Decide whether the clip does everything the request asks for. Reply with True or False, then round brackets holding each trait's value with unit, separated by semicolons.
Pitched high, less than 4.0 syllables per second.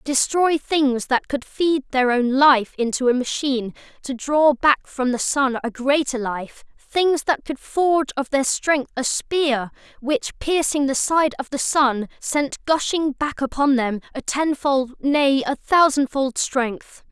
True (275 Hz; 3.8 syllables/s)